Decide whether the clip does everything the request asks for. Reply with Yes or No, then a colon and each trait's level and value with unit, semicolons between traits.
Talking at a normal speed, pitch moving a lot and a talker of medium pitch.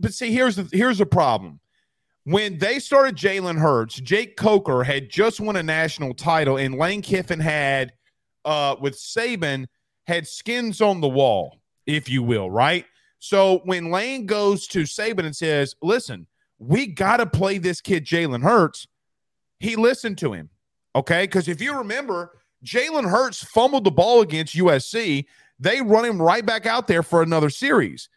Yes: average, 170 wpm; wide, 6.6 semitones; medium, 180 Hz